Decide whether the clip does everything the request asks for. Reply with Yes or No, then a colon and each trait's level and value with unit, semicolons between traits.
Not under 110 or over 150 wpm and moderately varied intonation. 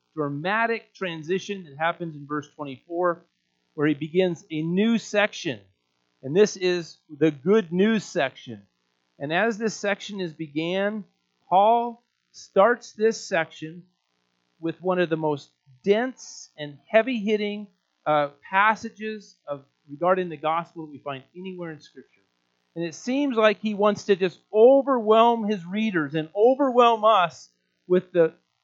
No: average, 140 wpm; wide, 6.2 semitones